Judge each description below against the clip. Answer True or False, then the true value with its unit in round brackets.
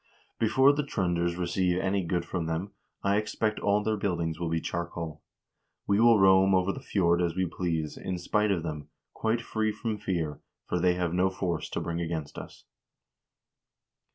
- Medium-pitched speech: False (90 Hz)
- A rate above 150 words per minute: True (180 wpm)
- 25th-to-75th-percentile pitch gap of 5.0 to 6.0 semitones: False (3.1 semitones)